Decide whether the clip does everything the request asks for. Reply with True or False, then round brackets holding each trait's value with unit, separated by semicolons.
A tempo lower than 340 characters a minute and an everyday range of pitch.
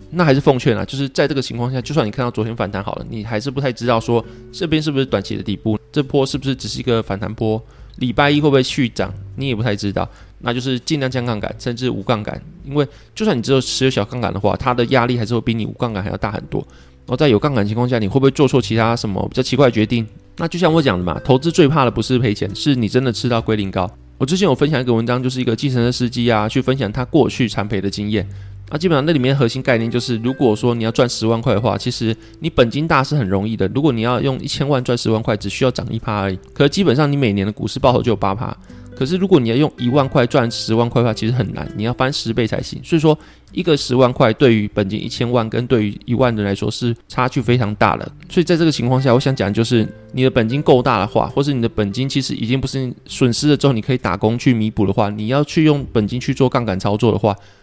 False (405 characters per minute; 3.8 semitones)